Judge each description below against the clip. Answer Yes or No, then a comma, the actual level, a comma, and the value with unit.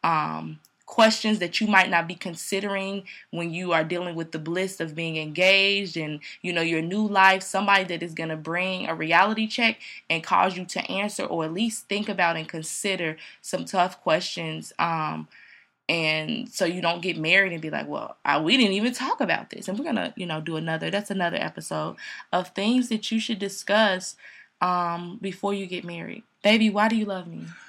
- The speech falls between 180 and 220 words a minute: Yes, average, 200 wpm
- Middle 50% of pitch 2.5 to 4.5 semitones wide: Yes, average, 3.4 semitones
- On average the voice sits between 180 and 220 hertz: Yes, medium, 185 Hz